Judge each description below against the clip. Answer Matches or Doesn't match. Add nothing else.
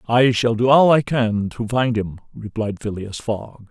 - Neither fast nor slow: Matches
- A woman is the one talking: Doesn't match